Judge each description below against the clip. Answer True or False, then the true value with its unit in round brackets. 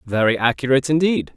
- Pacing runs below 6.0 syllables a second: False (6.4 syllables/s)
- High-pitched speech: False (135 Hz)